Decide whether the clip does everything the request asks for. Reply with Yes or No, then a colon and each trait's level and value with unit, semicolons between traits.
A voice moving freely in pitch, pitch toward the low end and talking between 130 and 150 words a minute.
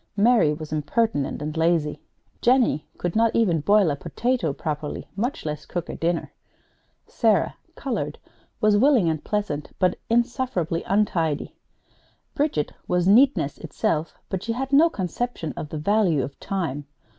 No: wide, 7.0 semitones; medium, 180 Hz; average, 145 wpm